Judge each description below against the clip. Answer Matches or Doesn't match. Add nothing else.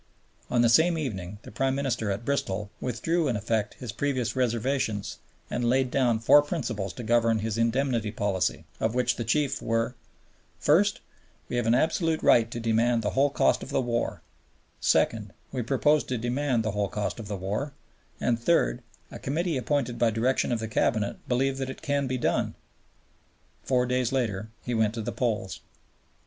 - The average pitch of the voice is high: Doesn't match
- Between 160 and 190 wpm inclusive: Matches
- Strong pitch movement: Doesn't match